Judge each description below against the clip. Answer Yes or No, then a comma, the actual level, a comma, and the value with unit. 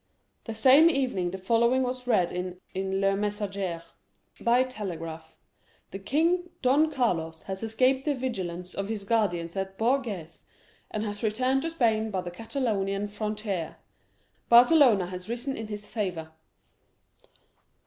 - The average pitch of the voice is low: No, high, 210 Hz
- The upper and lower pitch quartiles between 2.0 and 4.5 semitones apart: No, average, 4.9 semitones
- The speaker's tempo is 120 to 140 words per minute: Yes, slow, 135 wpm